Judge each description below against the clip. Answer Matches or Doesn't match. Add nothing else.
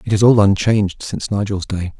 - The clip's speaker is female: Doesn't match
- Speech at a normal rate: Doesn't match